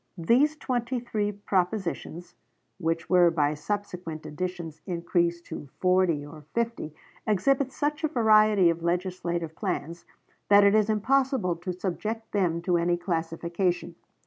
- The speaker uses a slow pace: Yes, slow, 130 wpm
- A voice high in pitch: No, medium, 180 Hz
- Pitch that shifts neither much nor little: Yes, average, 4.1 semitones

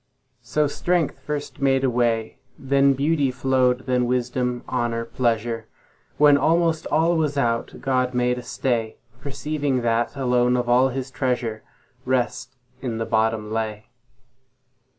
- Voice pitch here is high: No, low, 125 Hz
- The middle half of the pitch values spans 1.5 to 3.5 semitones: Yes, narrow, 2.6 semitones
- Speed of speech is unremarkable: No, slow, 120 wpm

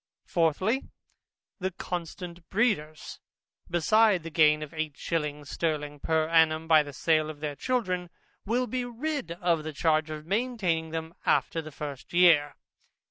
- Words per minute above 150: No, average, 145 wpm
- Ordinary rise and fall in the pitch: Yes, average, 3.0 semitones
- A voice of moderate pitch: Yes, medium, 165 Hz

